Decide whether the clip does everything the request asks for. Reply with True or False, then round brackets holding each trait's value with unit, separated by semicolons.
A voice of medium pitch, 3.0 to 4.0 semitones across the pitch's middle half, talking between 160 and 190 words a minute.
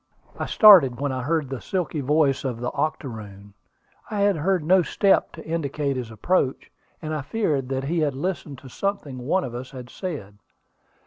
False (145 Hz; 5.0 semitones; 185 wpm)